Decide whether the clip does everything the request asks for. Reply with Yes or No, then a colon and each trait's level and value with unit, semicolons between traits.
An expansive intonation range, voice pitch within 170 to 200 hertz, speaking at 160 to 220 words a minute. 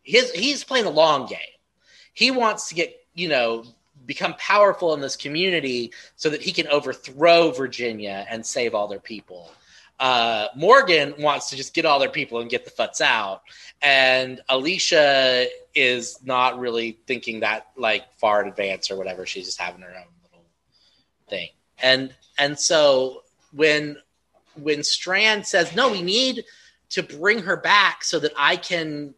No: wide, 6.2 semitones; medium, 140 Hz; average, 165 wpm